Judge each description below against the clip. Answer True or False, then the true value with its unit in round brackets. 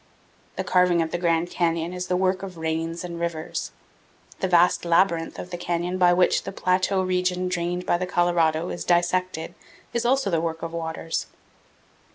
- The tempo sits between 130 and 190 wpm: True (175 wpm)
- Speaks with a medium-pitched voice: True (175 Hz)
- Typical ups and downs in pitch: False (1.5 semitones)